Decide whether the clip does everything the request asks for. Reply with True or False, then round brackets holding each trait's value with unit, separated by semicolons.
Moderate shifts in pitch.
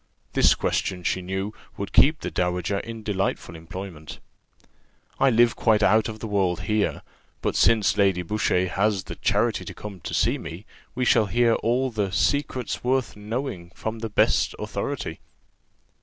True (3.6 semitones)